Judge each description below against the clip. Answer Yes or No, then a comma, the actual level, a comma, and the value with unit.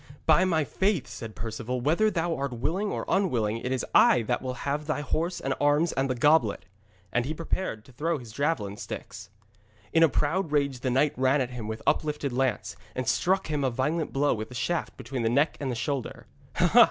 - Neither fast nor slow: No, fast, 210 wpm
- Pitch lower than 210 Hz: Yes, medium, 140 Hz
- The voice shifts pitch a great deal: No, average, 4.5 semitones